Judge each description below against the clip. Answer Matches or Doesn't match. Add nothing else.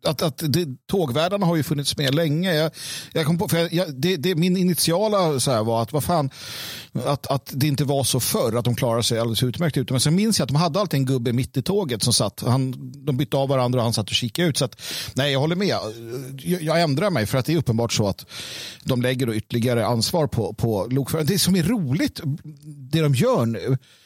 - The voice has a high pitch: Doesn't match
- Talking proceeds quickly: Matches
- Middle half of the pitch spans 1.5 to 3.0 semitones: Doesn't match